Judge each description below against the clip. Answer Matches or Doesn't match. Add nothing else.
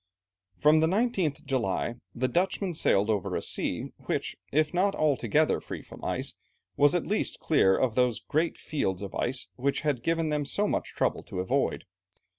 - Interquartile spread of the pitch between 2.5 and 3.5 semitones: Doesn't match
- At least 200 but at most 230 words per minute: Doesn't match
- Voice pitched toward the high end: Doesn't match